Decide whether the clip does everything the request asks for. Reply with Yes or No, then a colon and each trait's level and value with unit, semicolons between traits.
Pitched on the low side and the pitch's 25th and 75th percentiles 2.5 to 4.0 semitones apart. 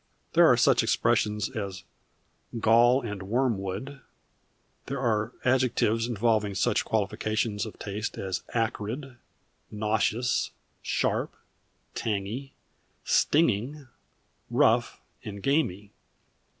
Yes: low, 110 Hz; average, 3.1 semitones